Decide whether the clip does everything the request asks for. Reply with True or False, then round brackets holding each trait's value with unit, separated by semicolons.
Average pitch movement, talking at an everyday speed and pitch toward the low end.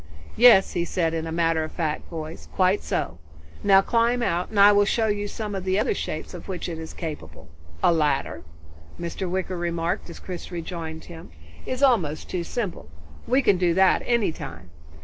False (3.9 semitones; 195 wpm; 175 Hz)